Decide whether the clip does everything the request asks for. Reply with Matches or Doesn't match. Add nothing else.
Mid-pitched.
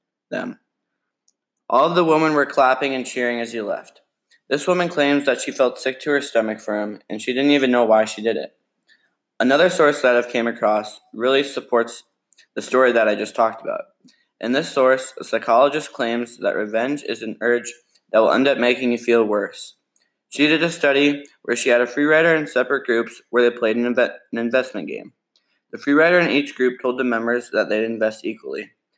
Doesn't match